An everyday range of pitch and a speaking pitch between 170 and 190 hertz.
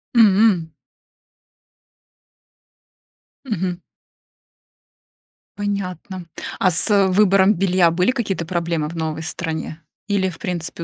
Yes: average, 3.0 semitones; medium, 185 Hz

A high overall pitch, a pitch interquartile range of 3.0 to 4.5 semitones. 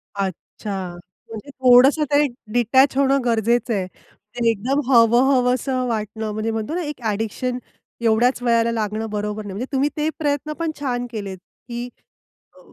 Yes: high, 235 Hz; average, 3.5 semitones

